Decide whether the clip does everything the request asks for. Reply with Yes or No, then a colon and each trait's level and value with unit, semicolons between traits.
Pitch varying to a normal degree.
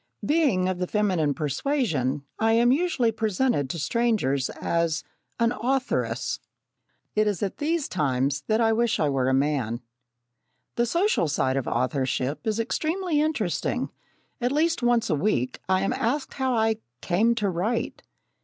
No: wide, 8.5 semitones